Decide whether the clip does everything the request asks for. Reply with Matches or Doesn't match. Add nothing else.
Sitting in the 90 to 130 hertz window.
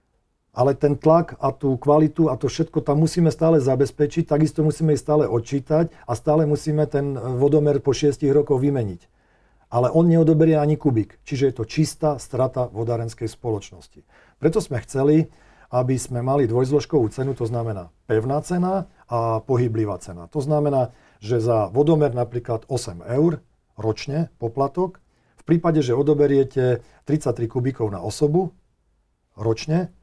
Doesn't match